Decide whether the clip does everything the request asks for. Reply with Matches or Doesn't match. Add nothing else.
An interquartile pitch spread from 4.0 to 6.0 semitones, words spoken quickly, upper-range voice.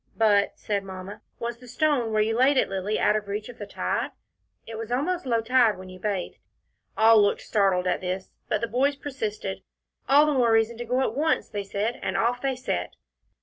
Doesn't match